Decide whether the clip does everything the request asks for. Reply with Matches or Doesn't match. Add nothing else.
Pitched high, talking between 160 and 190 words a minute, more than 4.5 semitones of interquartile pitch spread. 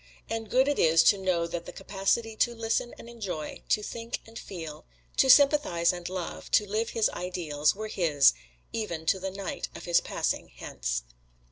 Matches